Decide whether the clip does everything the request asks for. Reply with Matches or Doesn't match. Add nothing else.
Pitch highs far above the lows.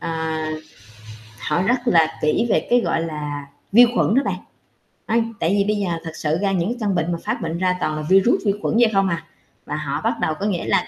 Doesn't match